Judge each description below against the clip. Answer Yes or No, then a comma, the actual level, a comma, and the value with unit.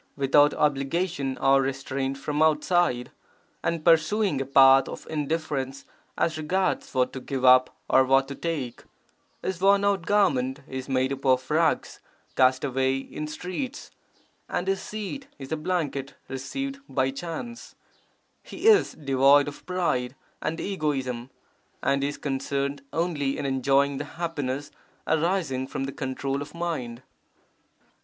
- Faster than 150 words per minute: No, average, 140 wpm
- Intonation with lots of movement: No, average, 4.0 semitones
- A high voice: No, medium, 140 Hz